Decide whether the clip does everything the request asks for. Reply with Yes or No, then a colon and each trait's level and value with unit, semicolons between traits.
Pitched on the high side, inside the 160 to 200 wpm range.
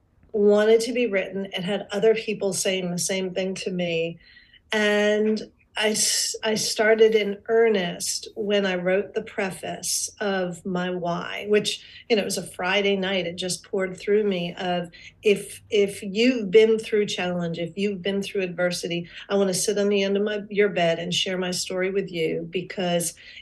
Yes: high, 200 Hz; average, 180 wpm